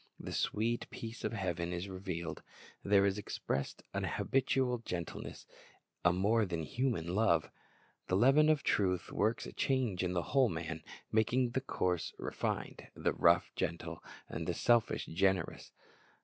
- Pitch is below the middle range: Yes, low, 100 Hz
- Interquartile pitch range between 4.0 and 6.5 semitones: Yes, average, 5.3 semitones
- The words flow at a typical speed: Yes, average, 145 wpm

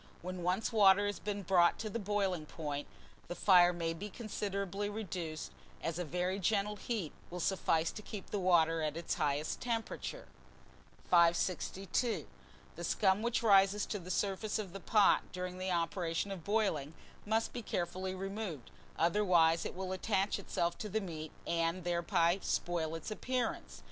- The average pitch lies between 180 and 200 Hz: Yes, medium, 185 Hz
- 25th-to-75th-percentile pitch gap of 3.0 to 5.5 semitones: Yes, average, 3.3 semitones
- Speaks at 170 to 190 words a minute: No, average, 160 wpm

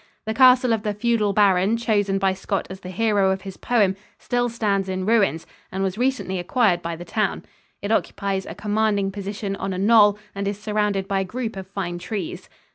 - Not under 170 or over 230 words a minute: Yes, average, 200 wpm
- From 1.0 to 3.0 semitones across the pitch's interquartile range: Yes, narrow, 2.4 semitones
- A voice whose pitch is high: Yes, high, 200 Hz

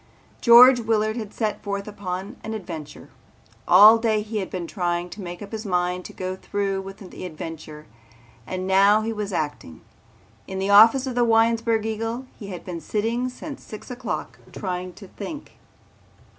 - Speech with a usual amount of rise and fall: Yes, average, 3.6 semitones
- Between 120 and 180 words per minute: Yes, average, 170 wpm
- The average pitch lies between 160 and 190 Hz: No, high, 205 Hz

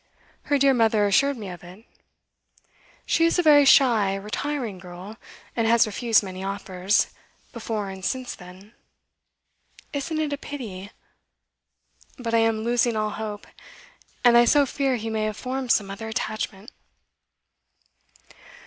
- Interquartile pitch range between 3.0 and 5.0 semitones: Yes, average, 4.3 semitones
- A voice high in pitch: Yes, high, 225 Hz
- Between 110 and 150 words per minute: Yes, average, 140 wpm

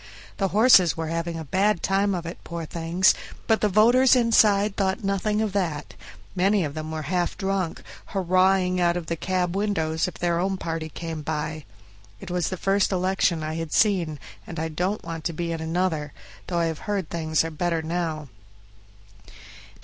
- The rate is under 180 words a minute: No, average, 185 wpm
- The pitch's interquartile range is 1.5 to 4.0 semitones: Yes, average, 3.1 semitones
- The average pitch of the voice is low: No, medium, 175 Hz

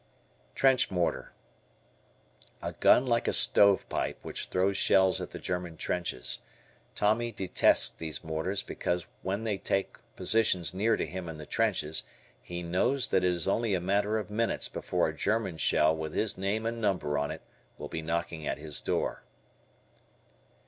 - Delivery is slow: No, average, 165 wpm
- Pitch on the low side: Yes, very low, 95 Hz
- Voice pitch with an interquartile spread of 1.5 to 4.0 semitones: No, average, 4.6 semitones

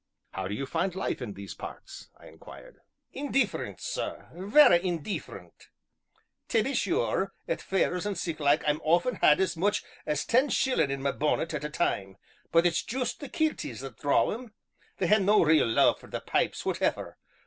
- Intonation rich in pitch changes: Yes, wide, 6.4 semitones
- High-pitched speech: No, medium, 175 Hz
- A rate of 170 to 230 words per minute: Yes, average, 180 wpm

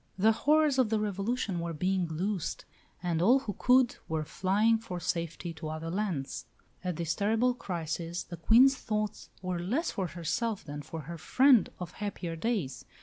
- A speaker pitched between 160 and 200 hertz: Yes, medium, 185 Hz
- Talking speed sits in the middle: Yes, average, 170 wpm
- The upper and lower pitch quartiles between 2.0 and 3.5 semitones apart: No, average, 5.2 semitones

